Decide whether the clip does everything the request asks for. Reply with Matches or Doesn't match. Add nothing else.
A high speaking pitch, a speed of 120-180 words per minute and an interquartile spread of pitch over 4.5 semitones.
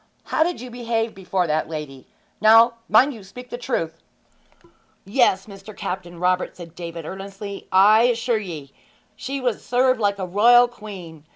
Matches